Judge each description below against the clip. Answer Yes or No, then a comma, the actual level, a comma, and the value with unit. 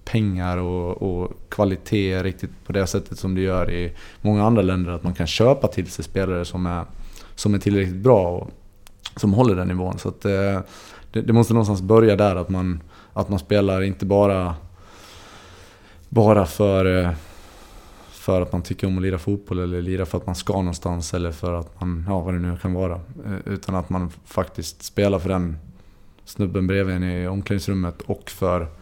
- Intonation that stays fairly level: Yes, narrow, 2.0 semitones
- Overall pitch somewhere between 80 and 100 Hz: Yes, very low, 95 Hz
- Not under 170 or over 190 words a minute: Yes, average, 185 wpm